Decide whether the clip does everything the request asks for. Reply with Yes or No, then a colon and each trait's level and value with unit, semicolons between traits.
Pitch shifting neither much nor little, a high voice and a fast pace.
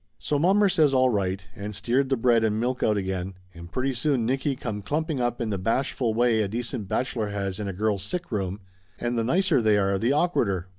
No: average, 4.5 semitones; low, 115 Hz; fast, 225 wpm